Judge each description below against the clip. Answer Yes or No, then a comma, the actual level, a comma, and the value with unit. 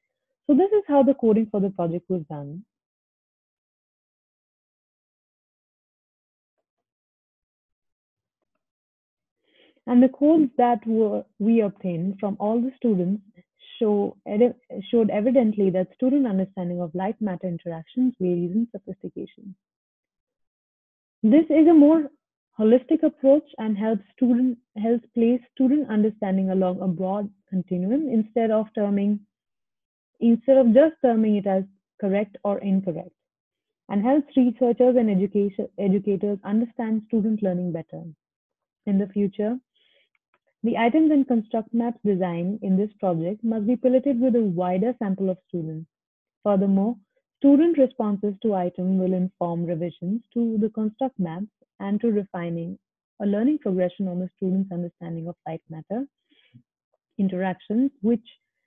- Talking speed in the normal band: No, slow, 125 wpm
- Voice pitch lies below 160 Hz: No, high, 210 Hz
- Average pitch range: Yes, average, 4.7 semitones